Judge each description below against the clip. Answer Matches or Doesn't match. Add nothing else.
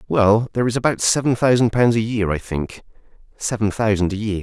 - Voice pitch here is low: Matches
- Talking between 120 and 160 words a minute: Doesn't match